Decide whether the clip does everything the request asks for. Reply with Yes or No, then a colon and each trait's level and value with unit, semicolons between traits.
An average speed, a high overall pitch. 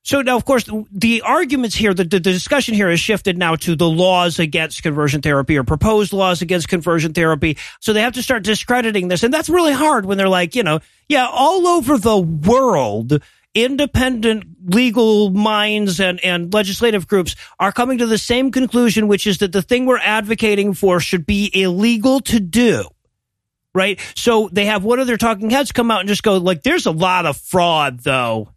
Yes: average, 195 wpm; high, 205 Hz